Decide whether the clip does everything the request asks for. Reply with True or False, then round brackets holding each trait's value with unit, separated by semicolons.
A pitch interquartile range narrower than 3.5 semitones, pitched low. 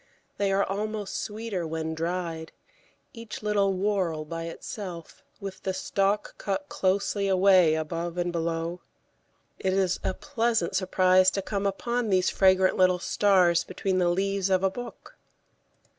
False (2.4 semitones; 190 Hz)